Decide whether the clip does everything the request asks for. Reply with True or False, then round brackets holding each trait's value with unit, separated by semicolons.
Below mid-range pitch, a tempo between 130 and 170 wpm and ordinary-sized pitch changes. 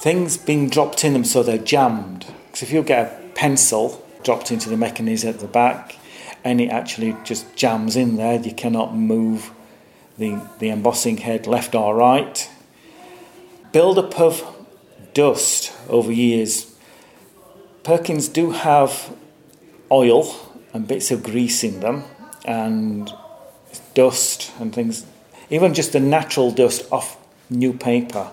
False (125 Hz; 140 wpm; 5.9 semitones)